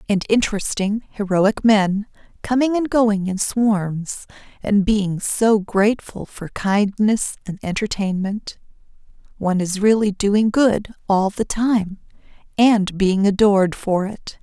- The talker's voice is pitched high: Yes, high, 205 Hz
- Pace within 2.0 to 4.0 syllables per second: Yes, 3.8 syllables/s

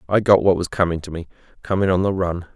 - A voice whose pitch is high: No, very low, 90 Hz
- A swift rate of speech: Yes, fast, 235 wpm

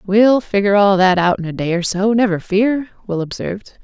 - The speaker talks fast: Yes, fast, 220 wpm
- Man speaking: No, female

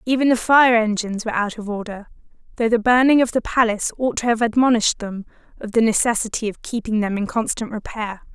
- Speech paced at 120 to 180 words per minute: No, average, 200 wpm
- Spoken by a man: No, female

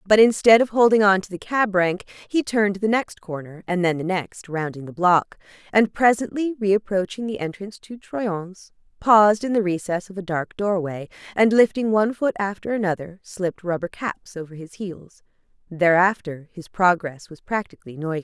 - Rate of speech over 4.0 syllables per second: Yes, 5.1 syllables/s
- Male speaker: No, female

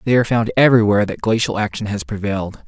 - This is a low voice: Yes, low, 110 Hz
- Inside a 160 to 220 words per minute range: Yes, average, 200 wpm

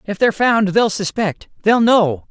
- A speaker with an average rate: Yes, average, 155 wpm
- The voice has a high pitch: Yes, high, 205 Hz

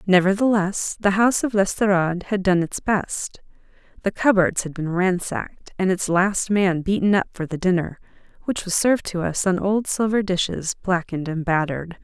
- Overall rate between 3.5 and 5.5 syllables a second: Yes, 5.1 syllables/s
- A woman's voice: Yes, female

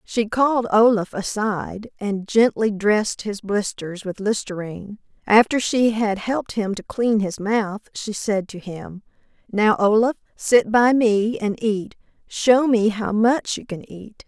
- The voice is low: No, high, 215 Hz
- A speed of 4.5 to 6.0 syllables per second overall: No, 4.1 syllables/s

